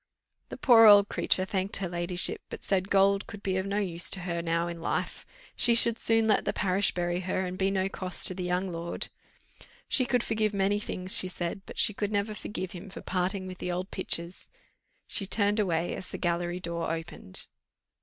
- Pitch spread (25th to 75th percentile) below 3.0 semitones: Yes, narrow, 2.4 semitones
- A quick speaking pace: Yes, fast, 210 wpm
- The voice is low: No, medium, 185 Hz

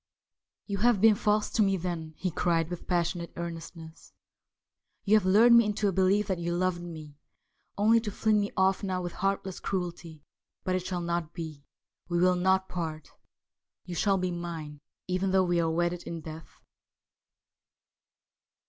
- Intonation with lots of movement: No, narrow, 2.5 semitones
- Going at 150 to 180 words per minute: Yes, average, 175 wpm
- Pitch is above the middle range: No, medium, 180 Hz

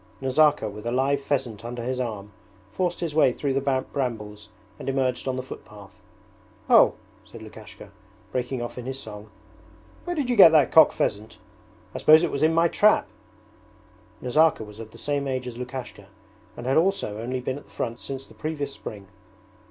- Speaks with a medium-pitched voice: No, low, 130 Hz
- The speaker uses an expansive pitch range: No, average, 3.9 semitones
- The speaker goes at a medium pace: Yes, average, 185 wpm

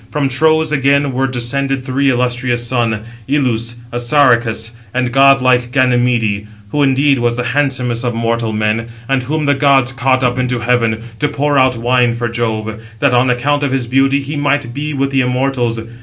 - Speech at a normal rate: Yes, average, 180 wpm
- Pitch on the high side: No, low, 125 Hz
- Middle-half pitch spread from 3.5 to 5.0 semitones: No, narrow, 2.5 semitones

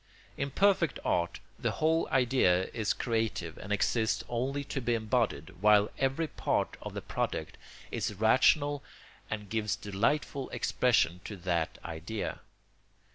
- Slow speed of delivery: Yes, slow, 130 wpm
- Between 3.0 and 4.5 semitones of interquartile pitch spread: No, average, 5.1 semitones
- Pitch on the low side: Yes, low, 110 Hz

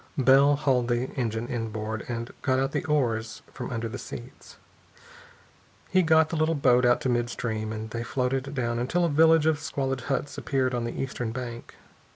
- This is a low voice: Yes, low, 125 Hz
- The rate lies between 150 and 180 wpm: No, average, 190 wpm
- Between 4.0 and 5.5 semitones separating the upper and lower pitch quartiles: No, average, 3.0 semitones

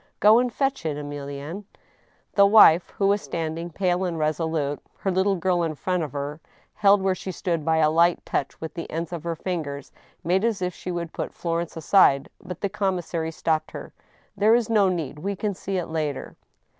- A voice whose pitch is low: No, medium, 170 Hz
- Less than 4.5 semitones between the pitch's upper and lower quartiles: Yes, average, 3.5 semitones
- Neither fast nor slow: No, fast, 210 wpm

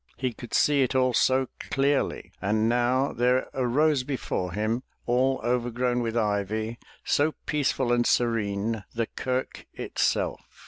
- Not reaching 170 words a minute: Yes, average, 140 wpm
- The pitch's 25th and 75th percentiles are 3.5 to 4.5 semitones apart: No, narrow, 2.5 semitones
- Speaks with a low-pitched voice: Yes, low, 120 Hz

